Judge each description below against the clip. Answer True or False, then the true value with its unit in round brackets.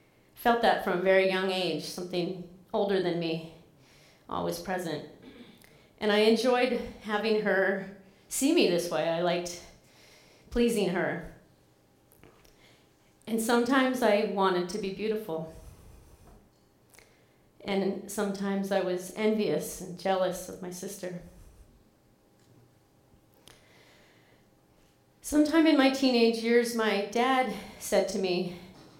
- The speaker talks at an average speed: False (110 wpm)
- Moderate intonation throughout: True (3.9 semitones)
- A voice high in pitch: True (195 Hz)